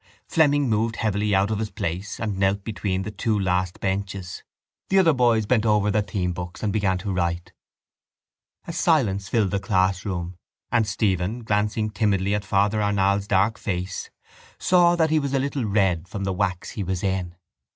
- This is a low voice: Yes, low, 100 Hz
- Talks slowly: No, average, 175 wpm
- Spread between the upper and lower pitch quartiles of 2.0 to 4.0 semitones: Yes, average, 2.7 semitones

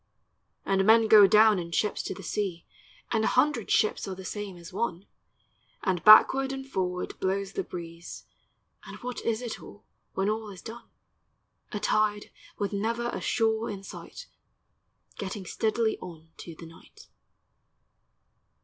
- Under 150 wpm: No, average, 155 wpm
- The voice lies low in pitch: No, high, 205 Hz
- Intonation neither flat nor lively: Yes, average, 3.0 semitones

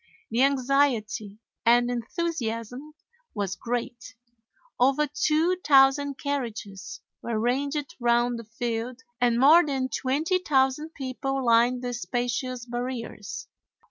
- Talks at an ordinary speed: No, slow, 100 wpm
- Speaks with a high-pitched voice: Yes, very high, 255 Hz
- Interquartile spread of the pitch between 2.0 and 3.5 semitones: Yes, average, 2.9 semitones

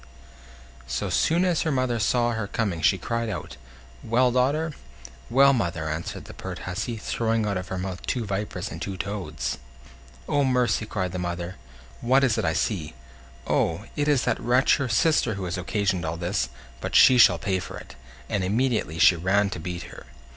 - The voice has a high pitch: No, low, 105 Hz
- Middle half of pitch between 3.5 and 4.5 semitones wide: No, wide, 5.4 semitones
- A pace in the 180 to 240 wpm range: Yes, average, 190 wpm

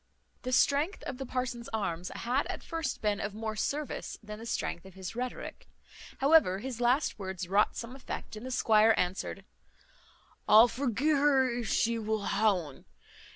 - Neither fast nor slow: Yes, average, 170 wpm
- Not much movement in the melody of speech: No, average, 4.1 semitones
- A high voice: Yes, high, 230 Hz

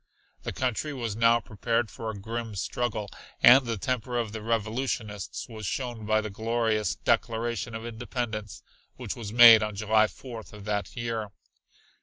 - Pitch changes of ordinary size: No, narrow, 1.7 semitones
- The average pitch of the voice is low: Yes, low, 115 Hz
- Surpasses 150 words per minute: Yes, average, 160 wpm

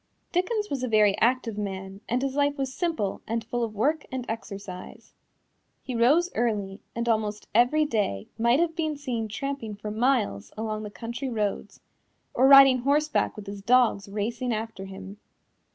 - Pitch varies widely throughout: No, average, 4.4 semitones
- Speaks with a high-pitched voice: Yes, high, 230 Hz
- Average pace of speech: Yes, average, 170 wpm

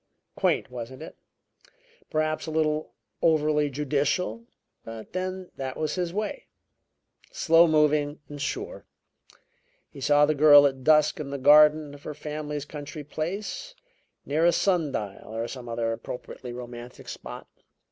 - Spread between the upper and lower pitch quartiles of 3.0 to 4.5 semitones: No, narrow, 2.4 semitones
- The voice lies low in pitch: No, medium, 150 Hz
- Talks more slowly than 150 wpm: Yes, average, 140 wpm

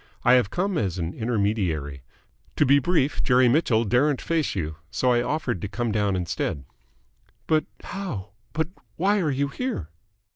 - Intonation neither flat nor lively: No, wide, 7.5 semitones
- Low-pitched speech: Yes, low, 125 Hz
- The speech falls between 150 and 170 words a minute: Yes, average, 160 wpm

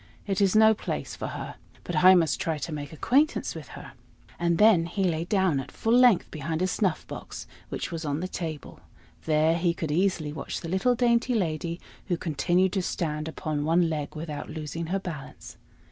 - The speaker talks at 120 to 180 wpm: No, average, 195 wpm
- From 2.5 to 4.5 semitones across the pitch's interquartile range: Yes, average, 3.4 semitones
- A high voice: No, medium, 170 Hz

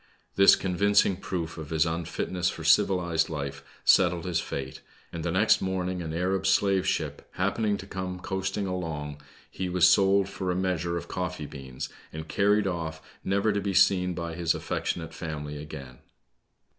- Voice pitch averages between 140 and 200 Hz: No, very low, 90 Hz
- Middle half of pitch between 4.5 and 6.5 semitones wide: No, average, 2.9 semitones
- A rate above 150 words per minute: Yes, average, 170 wpm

